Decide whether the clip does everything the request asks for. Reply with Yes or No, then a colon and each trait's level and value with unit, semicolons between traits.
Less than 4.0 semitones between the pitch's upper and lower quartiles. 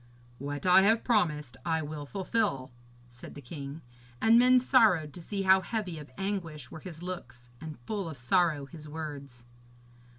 No: average, 5.1 semitones